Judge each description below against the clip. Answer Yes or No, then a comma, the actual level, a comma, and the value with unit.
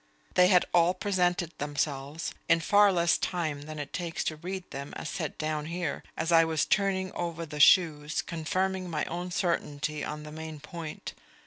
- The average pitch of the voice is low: No, medium, 165 Hz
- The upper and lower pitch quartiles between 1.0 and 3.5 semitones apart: Yes, average, 2.9 semitones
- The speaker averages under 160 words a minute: No, average, 180 wpm